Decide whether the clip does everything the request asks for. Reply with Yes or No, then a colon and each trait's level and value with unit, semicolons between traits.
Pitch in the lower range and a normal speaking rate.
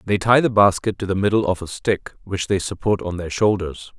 No: low, 100 Hz; fast, 240 wpm